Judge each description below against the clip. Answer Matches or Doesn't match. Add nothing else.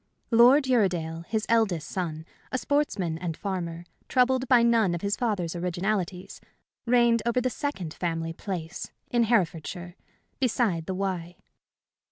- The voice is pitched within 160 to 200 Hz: Matches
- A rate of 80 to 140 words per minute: Matches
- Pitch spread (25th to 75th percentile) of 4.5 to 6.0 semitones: Matches